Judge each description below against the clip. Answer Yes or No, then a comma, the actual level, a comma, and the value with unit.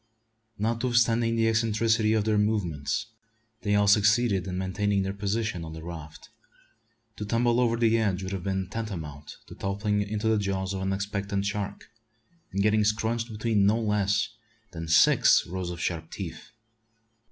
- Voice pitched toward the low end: Yes, low, 105 Hz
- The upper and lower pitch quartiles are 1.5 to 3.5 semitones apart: Yes, average, 2.7 semitones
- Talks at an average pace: Yes, average, 160 wpm